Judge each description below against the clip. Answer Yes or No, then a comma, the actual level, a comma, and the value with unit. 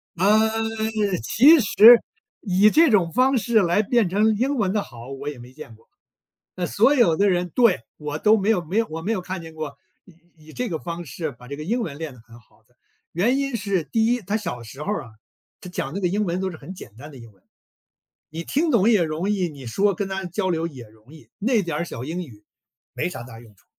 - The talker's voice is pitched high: No, medium, 180 Hz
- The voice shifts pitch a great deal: Yes, wide, 6.1 semitones